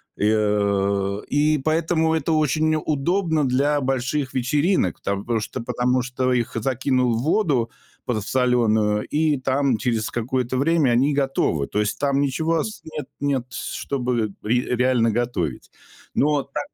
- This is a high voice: No, low, 130 Hz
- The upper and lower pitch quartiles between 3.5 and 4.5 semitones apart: Yes, average, 4.2 semitones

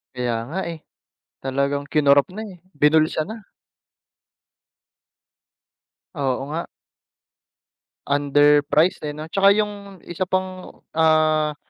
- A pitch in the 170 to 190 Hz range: No, medium, 155 Hz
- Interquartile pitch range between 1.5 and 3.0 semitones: No, average, 4.5 semitones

